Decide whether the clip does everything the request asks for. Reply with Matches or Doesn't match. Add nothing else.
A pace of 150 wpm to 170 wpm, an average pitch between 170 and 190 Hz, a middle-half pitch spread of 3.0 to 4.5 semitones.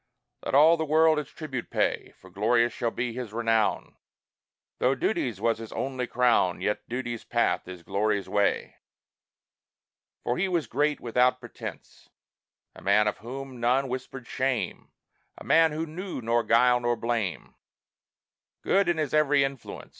Doesn't match